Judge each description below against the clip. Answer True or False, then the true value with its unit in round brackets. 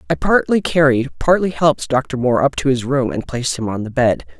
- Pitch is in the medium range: False (130 Hz)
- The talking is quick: True (230 wpm)